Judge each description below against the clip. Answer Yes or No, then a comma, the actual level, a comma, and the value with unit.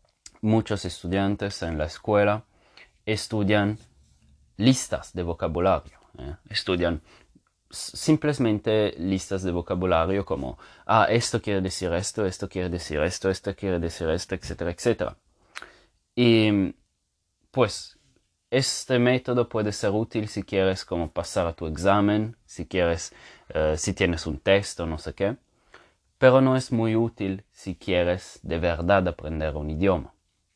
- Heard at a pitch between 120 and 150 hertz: No, very low, 95 Hz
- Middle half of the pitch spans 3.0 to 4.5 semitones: Yes, average, 3.8 semitones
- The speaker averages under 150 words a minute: Yes, slow, 135 wpm